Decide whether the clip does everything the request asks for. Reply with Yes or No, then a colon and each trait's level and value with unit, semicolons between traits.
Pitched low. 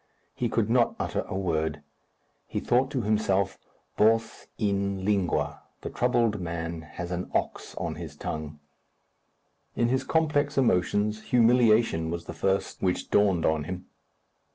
Yes: low, 100 Hz